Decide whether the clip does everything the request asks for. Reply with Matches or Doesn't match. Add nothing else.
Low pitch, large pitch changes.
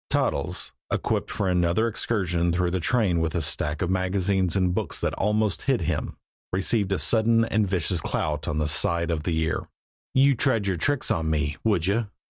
Doesn't match